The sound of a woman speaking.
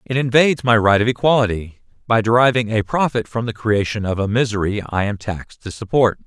No: male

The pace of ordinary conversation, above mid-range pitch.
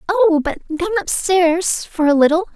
Yes: average, 165 wpm; very high, 345 Hz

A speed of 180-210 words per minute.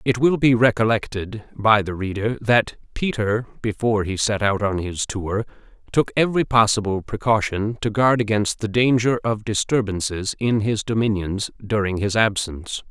No: average, 155 wpm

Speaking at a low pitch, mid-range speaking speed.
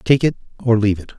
No: low, 115 Hz; fast, 255 wpm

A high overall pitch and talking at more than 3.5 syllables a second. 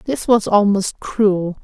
No: high, 205 Hz; 3.4 syllables/s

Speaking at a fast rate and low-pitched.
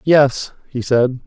No: average, 140 wpm; low, 130 Hz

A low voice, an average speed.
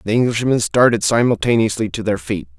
Yes: low, 105 Hz; average, 165 wpm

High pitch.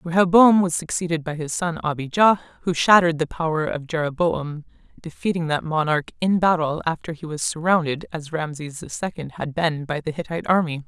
No: medium, 165 Hz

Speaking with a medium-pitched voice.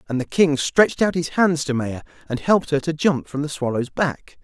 Yes: medium, 150 Hz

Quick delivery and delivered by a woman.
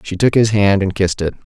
No: fast, 270 wpm; male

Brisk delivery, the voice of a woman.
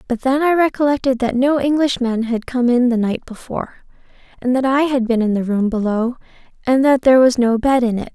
Yes: fast, 220 wpm; female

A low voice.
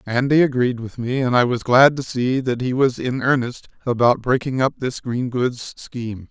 Yes: low, 125 Hz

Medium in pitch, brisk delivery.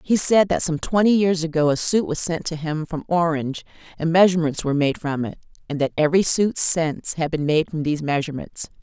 Yes: medium, 160 Hz; fast, 220 wpm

